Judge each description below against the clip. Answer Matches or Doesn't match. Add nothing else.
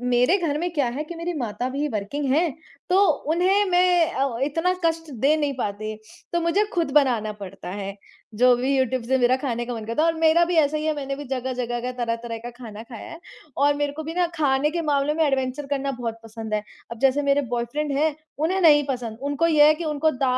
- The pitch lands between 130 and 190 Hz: Doesn't match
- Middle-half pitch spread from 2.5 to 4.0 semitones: Doesn't match